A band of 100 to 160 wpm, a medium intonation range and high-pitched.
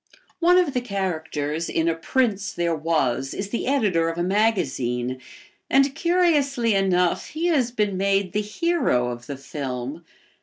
No: average, 155 wpm; wide, 8.0 semitones; high, 195 Hz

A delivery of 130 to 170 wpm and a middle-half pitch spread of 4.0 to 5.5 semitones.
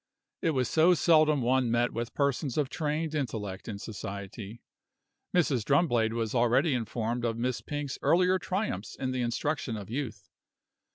Yes: average, 155 wpm; average, 4.7 semitones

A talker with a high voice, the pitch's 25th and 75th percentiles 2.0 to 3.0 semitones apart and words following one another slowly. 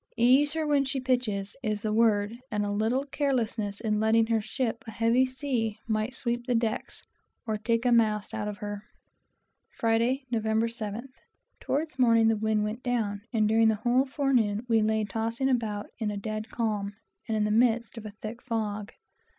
No: high, 225 Hz; narrow, 2.5 semitones; average, 185 wpm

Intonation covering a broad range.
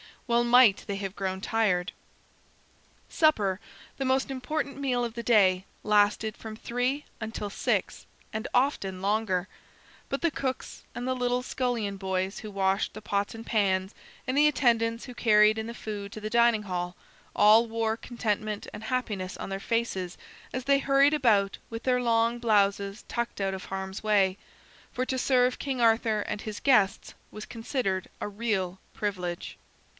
No: average, 3.8 semitones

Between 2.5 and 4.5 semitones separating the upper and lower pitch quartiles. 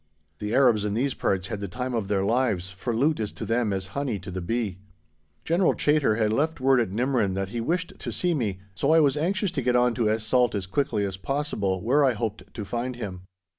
No: average, 5.1 semitones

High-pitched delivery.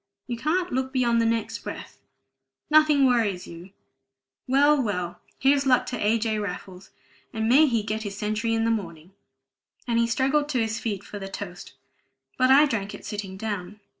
Yes: high, 225 Hz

